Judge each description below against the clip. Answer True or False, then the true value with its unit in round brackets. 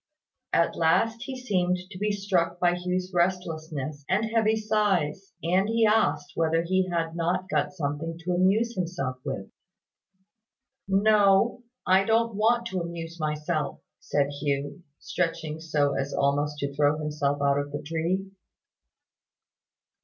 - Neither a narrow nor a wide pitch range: True (4.5 semitones)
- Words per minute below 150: True (140 wpm)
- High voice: False (175 Hz)